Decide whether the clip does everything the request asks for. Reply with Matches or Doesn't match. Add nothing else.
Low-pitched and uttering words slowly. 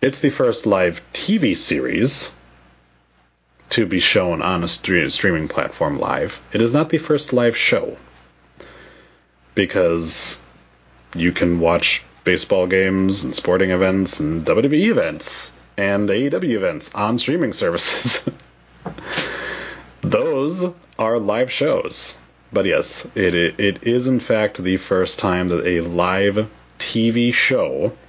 Matches